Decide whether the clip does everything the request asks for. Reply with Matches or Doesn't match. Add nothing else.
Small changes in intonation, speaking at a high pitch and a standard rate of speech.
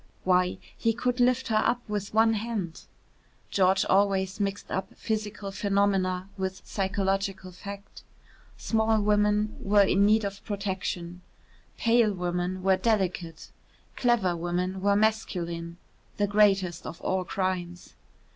Doesn't match